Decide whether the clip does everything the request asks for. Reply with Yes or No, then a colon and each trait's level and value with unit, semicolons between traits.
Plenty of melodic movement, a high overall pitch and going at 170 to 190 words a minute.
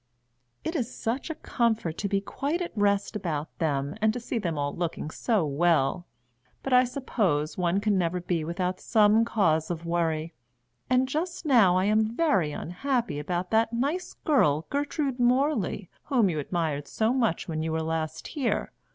Yes: wide, 7.2 semitones; high, 200 Hz; average, 175 wpm